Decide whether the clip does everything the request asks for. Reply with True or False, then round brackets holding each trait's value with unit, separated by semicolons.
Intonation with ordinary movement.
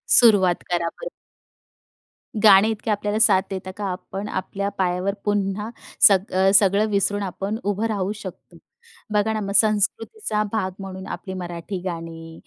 False (1.9 semitones)